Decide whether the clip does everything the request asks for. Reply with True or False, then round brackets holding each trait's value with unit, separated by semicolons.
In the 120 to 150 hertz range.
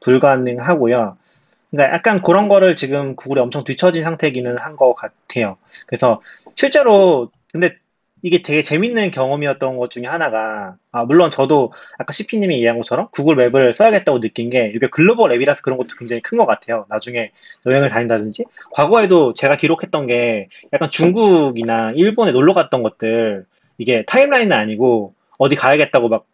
True (135 Hz)